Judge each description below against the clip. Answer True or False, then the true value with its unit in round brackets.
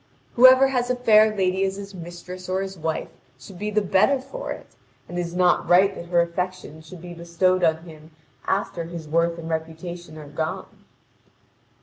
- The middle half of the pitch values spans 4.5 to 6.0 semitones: False (2.6 semitones)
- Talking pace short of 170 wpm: False (190 wpm)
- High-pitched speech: False (180 Hz)